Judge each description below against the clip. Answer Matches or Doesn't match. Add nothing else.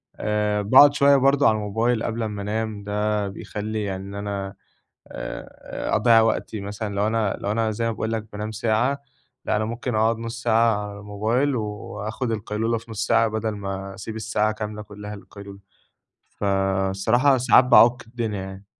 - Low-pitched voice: Matches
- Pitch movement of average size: Doesn't match